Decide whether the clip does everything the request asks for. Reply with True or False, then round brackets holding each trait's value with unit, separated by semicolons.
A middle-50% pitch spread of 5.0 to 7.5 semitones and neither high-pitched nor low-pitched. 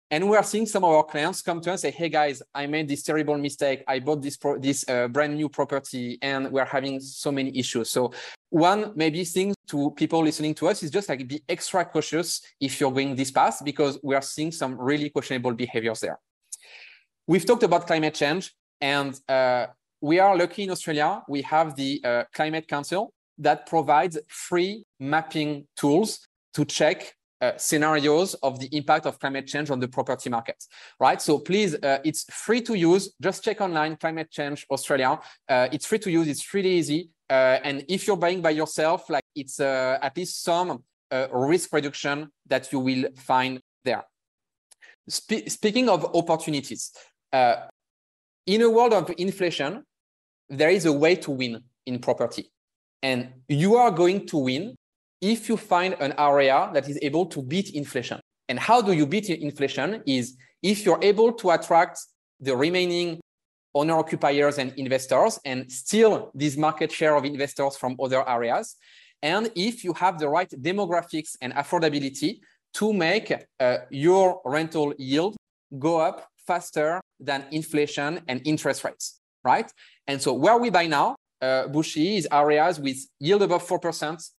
False (4.3 semitones; 150 Hz)